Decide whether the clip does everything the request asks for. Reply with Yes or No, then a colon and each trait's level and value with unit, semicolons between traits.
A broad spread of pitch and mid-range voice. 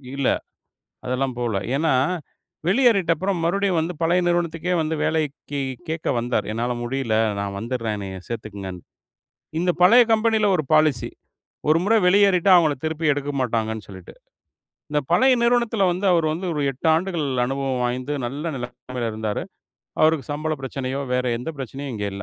Yes: wide, 6.1 semitones; medium, 145 Hz